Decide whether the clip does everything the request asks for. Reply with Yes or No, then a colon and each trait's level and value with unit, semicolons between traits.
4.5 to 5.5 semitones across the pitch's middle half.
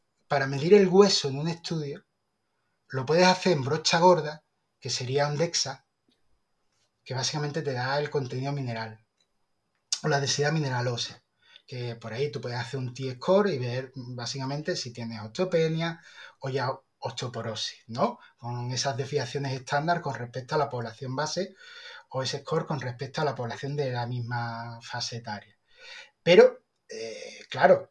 Yes: average, 5.1 semitones